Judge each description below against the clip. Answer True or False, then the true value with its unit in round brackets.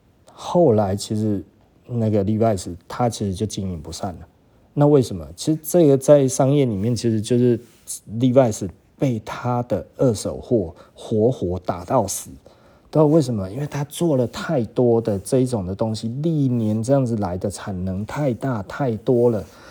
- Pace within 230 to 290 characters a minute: True (255 characters per minute)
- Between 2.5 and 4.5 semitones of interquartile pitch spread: False (5.0 semitones)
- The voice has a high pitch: False (115 Hz)